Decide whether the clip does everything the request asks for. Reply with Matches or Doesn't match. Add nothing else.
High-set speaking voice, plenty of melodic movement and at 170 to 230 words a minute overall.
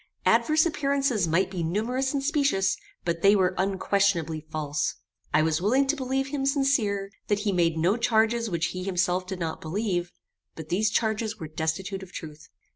Matches